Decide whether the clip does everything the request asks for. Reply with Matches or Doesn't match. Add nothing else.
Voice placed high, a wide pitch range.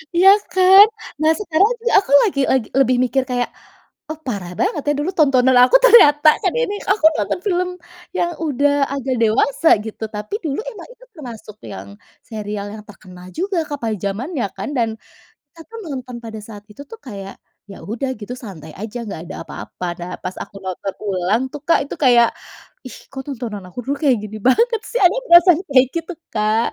Matches